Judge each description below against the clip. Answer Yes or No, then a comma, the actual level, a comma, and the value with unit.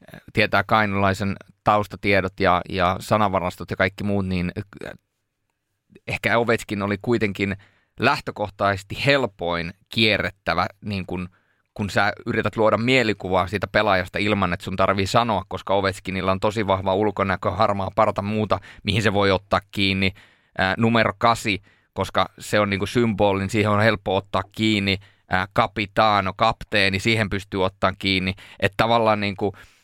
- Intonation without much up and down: Yes, narrow, 2.3 semitones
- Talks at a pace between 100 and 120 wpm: No, average, 140 wpm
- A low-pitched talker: Yes, low, 100 Hz